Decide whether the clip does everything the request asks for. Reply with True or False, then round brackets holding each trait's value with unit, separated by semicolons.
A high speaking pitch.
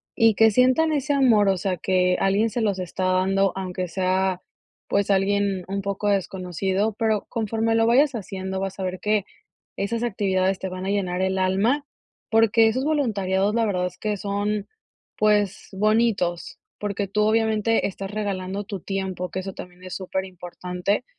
True (200 Hz)